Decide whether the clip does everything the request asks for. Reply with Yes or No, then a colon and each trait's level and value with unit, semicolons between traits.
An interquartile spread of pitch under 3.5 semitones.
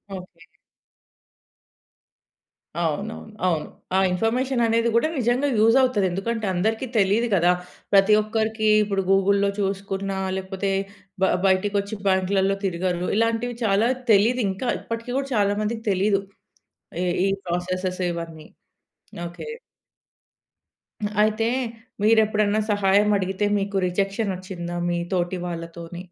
Yes: average, 3.1 semitones